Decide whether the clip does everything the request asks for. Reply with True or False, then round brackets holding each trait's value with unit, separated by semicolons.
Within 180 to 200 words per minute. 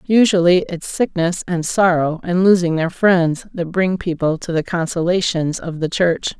False (170 wpm)